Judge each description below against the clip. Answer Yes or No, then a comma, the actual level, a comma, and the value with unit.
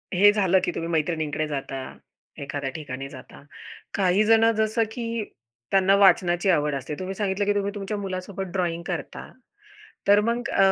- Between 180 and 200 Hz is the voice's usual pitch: Yes, high, 190 Hz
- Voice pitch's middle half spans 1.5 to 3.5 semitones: No, average, 4.4 semitones